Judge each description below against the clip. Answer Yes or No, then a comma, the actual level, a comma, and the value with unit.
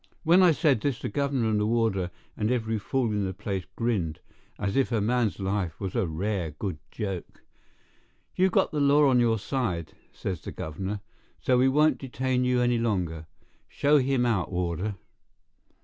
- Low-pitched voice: Yes, low, 110 Hz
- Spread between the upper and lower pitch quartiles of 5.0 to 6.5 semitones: Yes, average, 5.3 semitones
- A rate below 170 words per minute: No, average, 180 wpm